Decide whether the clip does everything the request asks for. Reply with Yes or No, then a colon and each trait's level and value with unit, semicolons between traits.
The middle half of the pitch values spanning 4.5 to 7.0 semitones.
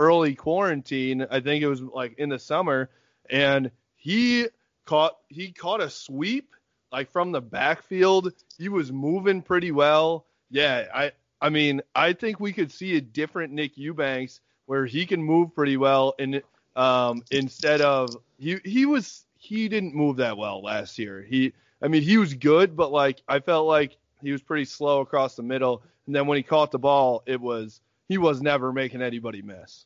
No: average, 4.1 semitones